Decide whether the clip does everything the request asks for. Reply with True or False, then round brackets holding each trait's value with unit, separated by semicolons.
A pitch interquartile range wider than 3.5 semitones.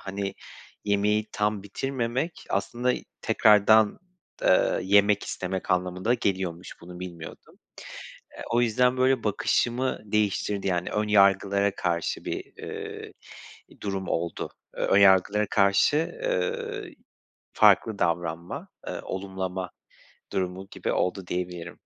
False (3.1 semitones)